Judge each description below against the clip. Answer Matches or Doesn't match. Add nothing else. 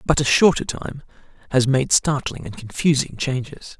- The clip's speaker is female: Doesn't match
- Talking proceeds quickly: Doesn't match